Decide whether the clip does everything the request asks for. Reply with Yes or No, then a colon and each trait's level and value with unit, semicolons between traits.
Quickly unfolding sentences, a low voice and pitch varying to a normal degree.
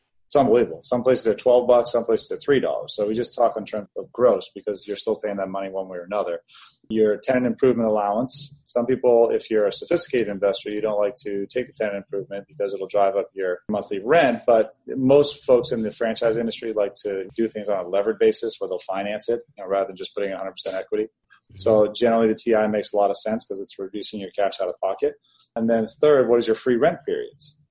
No: fast, 235 wpm; low, 115 Hz; wide, 6.3 semitones